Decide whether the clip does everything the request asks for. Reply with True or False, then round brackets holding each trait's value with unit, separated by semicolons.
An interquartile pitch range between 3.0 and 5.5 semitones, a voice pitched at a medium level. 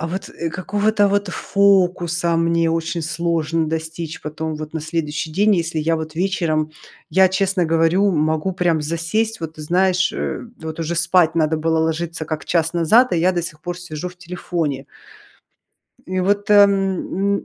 False (2.6 semitones; 170 Hz)